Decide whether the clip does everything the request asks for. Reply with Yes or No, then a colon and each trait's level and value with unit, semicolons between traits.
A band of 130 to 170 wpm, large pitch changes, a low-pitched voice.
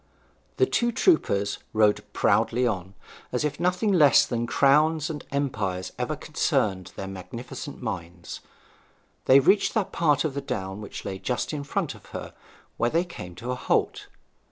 Yes: average, 160 wpm; wide, 7.6 semitones; low, 125 Hz